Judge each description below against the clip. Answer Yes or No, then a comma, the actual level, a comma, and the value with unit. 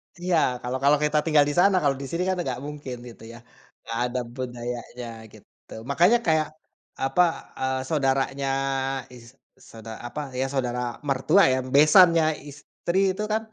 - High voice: No, medium, 140 Hz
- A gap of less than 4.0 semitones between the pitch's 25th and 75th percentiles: No, average, 4.3 semitones